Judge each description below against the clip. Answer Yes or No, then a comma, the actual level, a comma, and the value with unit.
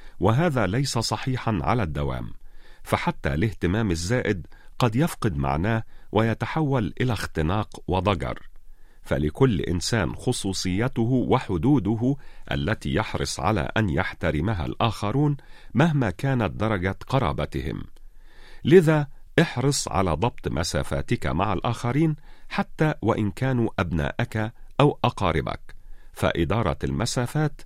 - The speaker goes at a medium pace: Yes, average, 95 wpm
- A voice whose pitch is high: No, low, 115 Hz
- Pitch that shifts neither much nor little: No, wide, 6.5 semitones